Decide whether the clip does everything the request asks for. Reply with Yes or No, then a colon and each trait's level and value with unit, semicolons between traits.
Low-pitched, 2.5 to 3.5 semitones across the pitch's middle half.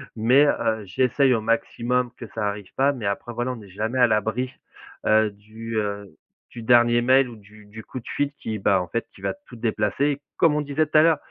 Yes: low, 115 Hz; average, 3.2 semitones